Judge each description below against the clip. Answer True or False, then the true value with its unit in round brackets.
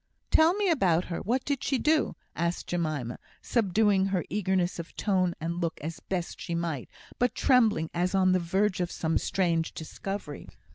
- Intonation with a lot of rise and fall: False (3.7 semitones)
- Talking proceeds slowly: False (175 wpm)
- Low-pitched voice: False (185 Hz)